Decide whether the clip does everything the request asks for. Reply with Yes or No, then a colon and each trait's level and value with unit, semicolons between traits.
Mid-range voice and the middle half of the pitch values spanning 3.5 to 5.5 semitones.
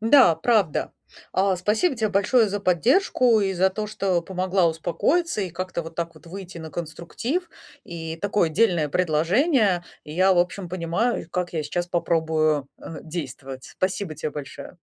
Yes: medium, 180 Hz; average, 3.9 semitones